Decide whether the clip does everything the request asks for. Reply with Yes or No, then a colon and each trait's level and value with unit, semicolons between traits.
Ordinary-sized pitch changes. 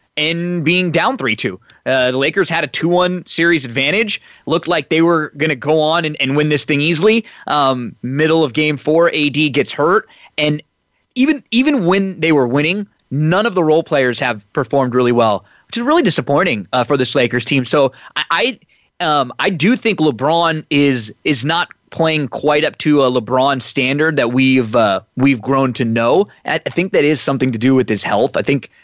Yes: average, 4.1 semitones